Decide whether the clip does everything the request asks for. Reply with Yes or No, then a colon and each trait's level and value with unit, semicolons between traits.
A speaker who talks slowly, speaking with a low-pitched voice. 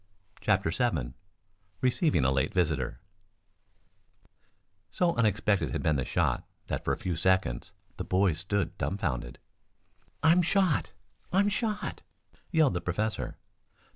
Yes: slow, 120 wpm; low, 100 Hz